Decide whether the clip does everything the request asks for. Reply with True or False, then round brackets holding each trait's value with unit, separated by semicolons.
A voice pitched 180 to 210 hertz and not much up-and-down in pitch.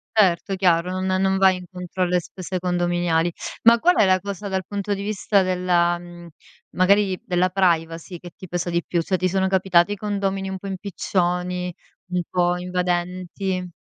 True (185 Hz; 1.6 semitones)